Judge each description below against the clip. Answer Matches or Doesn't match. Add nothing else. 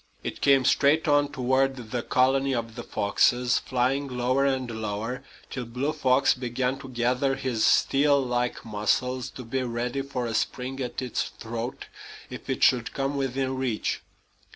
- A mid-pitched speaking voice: Doesn't match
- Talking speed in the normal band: Matches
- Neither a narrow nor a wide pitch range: Doesn't match